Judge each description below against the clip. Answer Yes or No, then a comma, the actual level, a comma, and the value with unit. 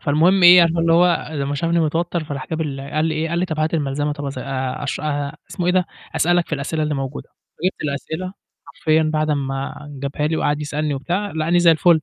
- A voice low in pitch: No, medium, 155 Hz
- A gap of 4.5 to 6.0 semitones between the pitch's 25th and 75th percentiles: No, average, 2.8 semitones